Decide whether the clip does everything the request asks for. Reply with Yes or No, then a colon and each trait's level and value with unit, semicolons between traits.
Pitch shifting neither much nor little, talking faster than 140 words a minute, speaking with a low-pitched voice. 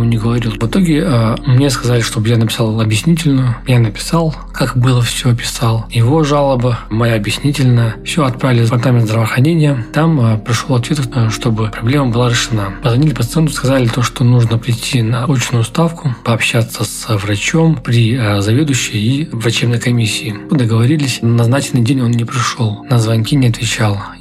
Yes: average, 3.2 semitones; average, 155 wpm; low, 120 Hz